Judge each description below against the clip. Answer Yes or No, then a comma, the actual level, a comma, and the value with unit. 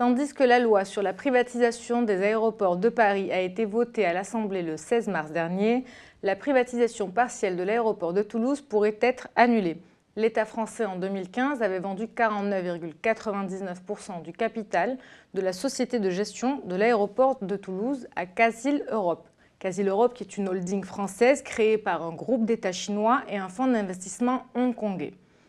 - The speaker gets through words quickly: No, average, 160 wpm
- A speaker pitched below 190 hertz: No, high, 215 Hz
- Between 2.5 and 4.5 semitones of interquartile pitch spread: Yes, average, 3.7 semitones